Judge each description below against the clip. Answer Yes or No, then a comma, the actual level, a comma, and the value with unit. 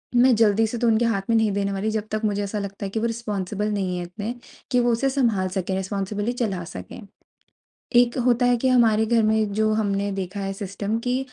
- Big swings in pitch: No, average, 2.7 semitones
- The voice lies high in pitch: Yes, high, 215 Hz